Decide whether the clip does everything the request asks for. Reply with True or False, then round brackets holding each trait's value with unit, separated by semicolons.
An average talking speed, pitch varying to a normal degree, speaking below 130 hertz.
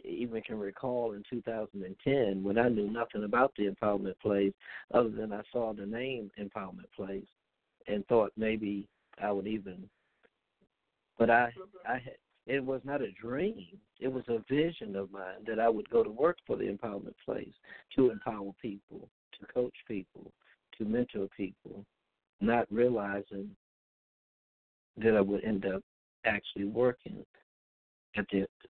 True (150 wpm; 3.6 semitones; 110 Hz)